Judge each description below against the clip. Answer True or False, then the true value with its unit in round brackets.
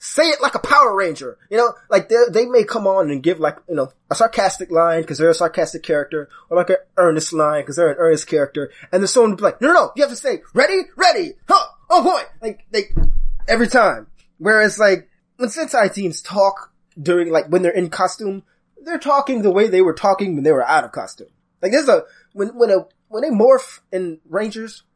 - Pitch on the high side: True (200 Hz)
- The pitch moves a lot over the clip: True (8.2 semitones)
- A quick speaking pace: True (225 wpm)